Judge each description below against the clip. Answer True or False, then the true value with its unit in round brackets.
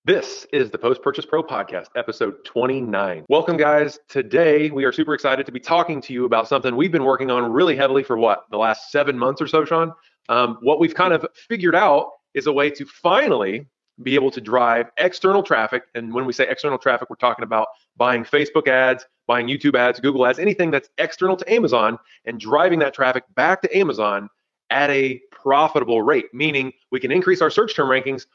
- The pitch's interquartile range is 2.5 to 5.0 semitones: True (4.3 semitones)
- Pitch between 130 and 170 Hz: True (140 Hz)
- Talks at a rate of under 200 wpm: False (205 wpm)